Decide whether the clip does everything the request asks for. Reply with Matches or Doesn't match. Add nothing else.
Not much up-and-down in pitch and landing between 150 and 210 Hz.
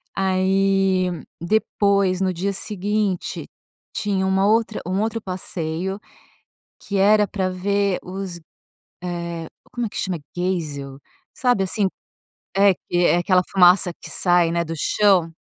Matches